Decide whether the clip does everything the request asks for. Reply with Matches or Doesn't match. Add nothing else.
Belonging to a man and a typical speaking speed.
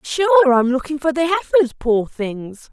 Doesn't match